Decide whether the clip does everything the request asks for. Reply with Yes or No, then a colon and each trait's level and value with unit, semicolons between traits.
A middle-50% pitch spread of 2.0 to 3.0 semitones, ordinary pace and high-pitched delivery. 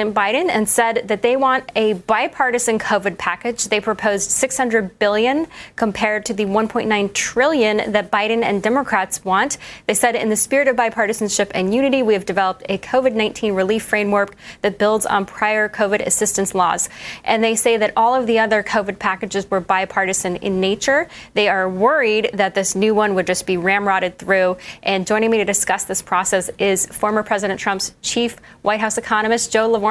Yes: narrow, 2.4 semitones; average, 185 wpm; high, 215 Hz